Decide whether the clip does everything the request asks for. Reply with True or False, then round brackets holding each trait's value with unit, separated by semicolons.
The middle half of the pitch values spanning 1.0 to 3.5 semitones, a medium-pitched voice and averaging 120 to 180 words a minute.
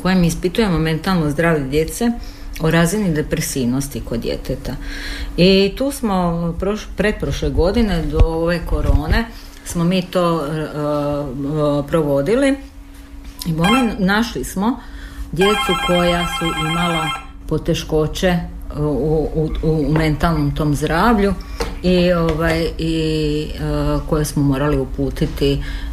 False (3.2 semitones; 160 Hz; 110 wpm)